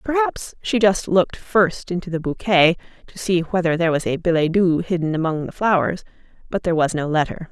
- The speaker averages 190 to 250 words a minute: Yes, average, 200 wpm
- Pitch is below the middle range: No, medium, 175 Hz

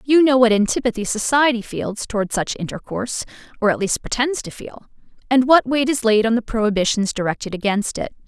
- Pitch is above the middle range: Yes, high, 230 Hz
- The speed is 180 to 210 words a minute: Yes, average, 190 wpm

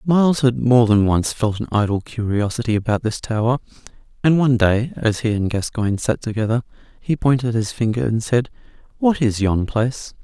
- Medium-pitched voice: No, low, 115 Hz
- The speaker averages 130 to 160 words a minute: No, average, 180 wpm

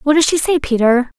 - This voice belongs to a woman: Yes, female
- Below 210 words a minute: No, fast, 255 wpm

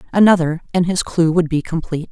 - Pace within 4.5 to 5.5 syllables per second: No, 6.3 syllables/s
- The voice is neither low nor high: Yes, medium, 170 Hz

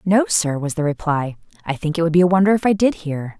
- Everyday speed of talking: No, fast, 285 wpm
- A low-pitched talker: No, medium, 165 Hz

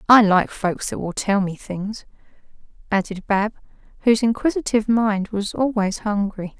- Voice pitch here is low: No, high, 210 Hz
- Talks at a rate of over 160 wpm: No, average, 145 wpm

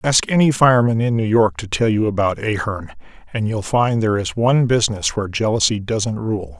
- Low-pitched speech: Yes, low, 110 Hz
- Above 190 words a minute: Yes, average, 200 wpm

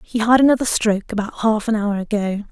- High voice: Yes, high, 215 Hz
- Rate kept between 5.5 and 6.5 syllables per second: Yes, 6.0 syllables/s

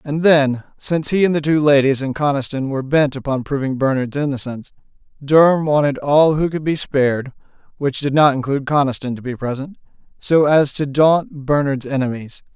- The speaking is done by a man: Yes, male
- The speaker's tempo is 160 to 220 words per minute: Yes, average, 170 wpm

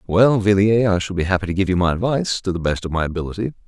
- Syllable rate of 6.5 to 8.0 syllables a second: Yes, 7.2 syllables/s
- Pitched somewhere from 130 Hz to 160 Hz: No, very low, 95 Hz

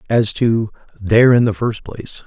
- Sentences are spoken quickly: No, average, 185 wpm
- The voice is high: No, low, 110 Hz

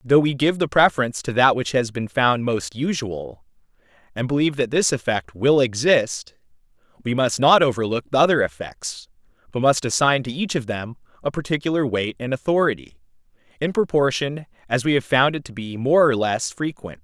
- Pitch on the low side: Yes, low, 125 Hz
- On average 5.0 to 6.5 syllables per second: Yes, 5.3 syllables/s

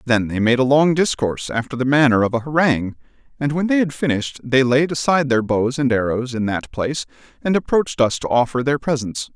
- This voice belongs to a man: Yes, male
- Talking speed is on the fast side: Yes, fast, 220 wpm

